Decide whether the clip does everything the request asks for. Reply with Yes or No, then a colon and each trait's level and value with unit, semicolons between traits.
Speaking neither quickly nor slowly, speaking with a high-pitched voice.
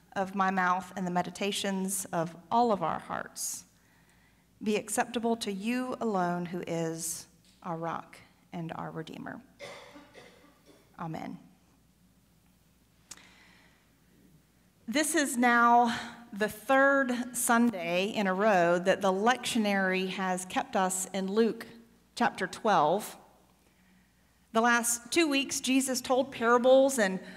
No: slow, 110 wpm; high, 215 Hz